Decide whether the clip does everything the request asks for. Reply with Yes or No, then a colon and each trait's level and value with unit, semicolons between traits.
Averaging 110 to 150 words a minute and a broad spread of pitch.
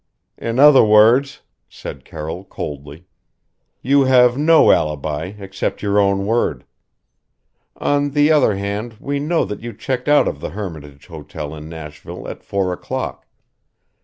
Yes: average, 140 wpm; wide, 8.8 semitones